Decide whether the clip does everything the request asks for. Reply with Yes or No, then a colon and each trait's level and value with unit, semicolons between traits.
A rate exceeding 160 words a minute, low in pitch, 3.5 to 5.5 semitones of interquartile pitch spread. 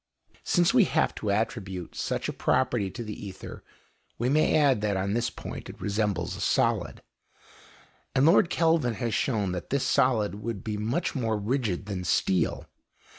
Yes: average, 170 wpm; low, 110 Hz; average, 4.5 semitones